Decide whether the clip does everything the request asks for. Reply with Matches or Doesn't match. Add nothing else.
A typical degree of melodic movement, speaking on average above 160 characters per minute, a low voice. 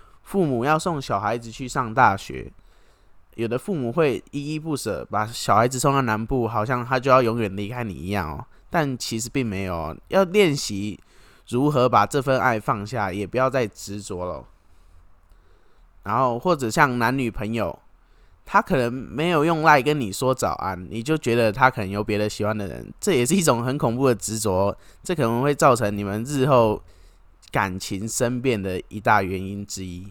Matches